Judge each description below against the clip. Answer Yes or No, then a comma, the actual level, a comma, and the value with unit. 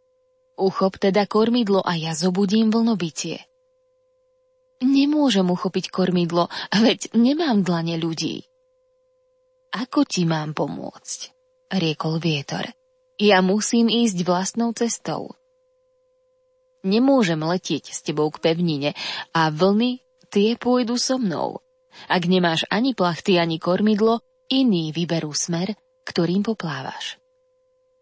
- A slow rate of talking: Yes, slow, 105 wpm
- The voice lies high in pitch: Yes, high, 220 Hz